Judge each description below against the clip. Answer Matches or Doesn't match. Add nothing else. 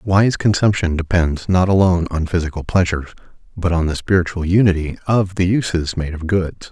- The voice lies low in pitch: Matches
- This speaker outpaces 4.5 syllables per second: Matches